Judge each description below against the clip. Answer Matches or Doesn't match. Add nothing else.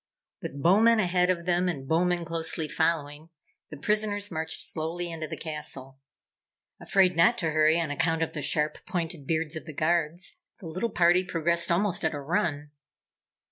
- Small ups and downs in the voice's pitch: Matches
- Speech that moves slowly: Doesn't match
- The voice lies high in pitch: Doesn't match